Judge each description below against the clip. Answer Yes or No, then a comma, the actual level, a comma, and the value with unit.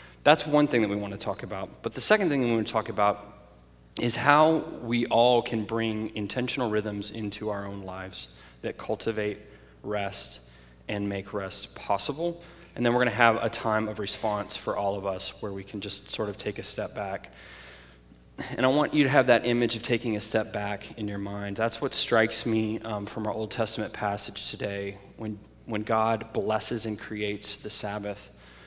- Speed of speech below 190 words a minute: No, fast, 205 wpm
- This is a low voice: Yes, low, 105 Hz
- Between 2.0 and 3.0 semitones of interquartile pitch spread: Yes, narrow, 2.4 semitones